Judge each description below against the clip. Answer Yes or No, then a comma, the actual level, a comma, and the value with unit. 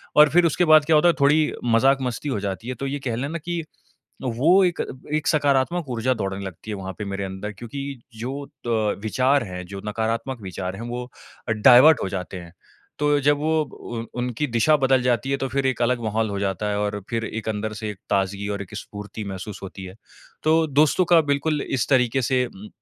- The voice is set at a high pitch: No, low, 125 Hz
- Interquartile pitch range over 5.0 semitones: Yes, wide, 5.5 semitones